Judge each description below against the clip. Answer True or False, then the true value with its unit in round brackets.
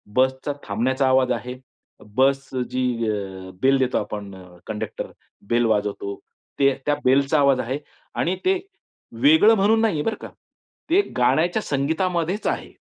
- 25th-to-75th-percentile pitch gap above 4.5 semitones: True (5.6 semitones)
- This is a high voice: False (135 Hz)